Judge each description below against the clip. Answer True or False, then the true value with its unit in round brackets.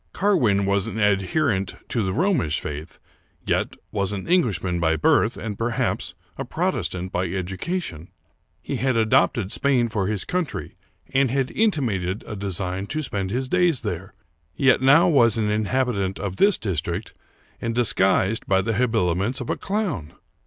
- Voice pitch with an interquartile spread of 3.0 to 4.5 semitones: False (5.6 semitones)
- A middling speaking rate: True (160 wpm)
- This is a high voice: False (105 Hz)